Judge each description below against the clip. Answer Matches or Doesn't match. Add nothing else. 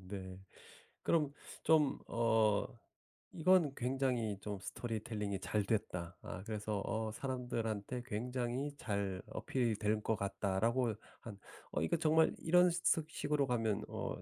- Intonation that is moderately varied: Matches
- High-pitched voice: Doesn't match